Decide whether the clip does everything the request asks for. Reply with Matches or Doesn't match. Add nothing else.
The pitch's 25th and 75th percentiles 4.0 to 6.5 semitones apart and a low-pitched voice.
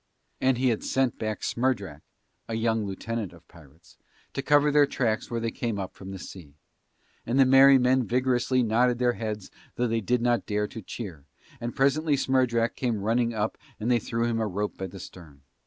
Doesn't match